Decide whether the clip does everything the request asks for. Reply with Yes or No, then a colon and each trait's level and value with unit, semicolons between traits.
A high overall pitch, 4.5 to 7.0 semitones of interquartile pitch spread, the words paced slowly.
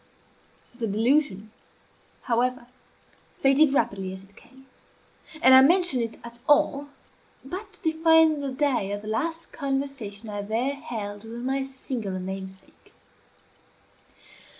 Yes: very high, 255 Hz; average, 5.2 semitones; slow, 125 wpm